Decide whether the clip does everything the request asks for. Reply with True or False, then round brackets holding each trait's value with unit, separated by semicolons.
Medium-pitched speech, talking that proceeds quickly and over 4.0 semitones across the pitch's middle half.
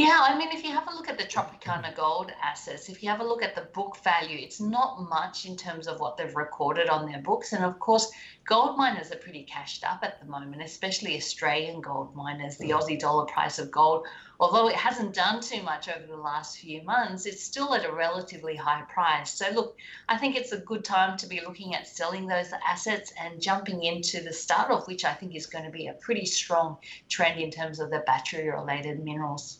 True (170 Hz; 230 wpm; 4.8 semitones)